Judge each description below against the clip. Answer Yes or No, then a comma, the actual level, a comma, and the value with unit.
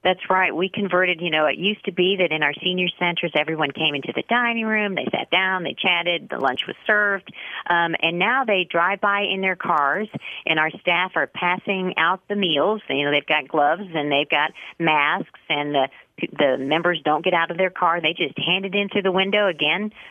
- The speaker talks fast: Yes, fast, 225 wpm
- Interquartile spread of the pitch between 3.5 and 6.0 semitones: Yes, average, 3.9 semitones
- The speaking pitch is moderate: Yes, medium, 180 Hz